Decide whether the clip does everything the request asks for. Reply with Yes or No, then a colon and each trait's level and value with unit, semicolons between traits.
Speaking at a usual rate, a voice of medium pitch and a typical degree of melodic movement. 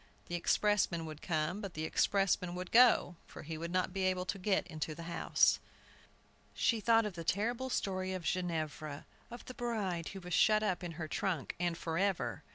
Yes: average, 190 wpm; medium, 180 Hz; average, 3.4 semitones